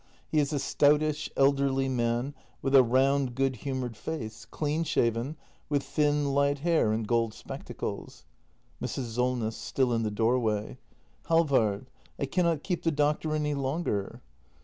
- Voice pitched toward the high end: No, low, 135 Hz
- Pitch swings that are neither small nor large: Yes, average, 4.1 semitones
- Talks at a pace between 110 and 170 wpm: Yes, average, 145 wpm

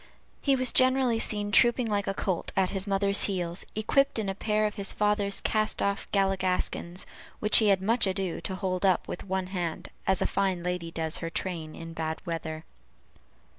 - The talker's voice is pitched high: Yes, high, 195 Hz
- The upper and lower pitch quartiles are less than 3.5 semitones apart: Yes, average, 2.8 semitones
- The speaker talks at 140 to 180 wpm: No, average, 190 wpm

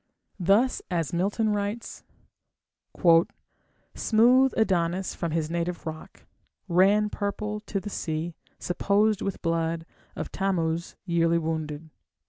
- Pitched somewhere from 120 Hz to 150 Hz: No, medium, 180 Hz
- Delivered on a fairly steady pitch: No, average, 3.9 semitones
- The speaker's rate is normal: No, slow, 105 wpm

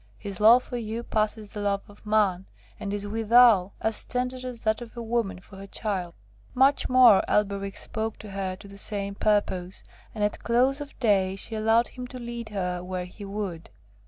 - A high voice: Yes, high, 210 Hz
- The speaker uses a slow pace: No, average, 195 wpm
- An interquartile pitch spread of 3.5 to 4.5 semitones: No, average, 3.0 semitones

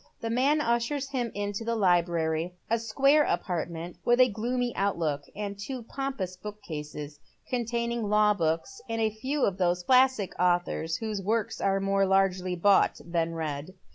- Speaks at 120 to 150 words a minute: No, average, 160 wpm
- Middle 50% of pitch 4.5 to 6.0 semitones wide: Yes, average, 5.1 semitones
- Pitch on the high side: Yes, high, 200 Hz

